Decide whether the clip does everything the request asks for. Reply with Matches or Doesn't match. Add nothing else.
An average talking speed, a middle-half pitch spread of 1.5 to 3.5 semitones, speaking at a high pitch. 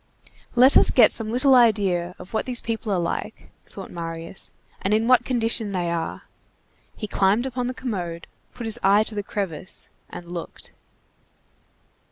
Doesn't match